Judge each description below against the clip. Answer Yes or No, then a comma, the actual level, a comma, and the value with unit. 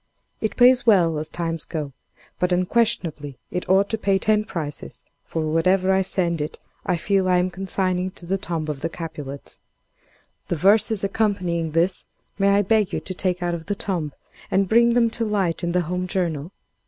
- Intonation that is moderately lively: Yes, average, 3.1 semitones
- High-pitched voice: No, medium, 180 Hz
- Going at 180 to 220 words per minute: Yes, average, 190 wpm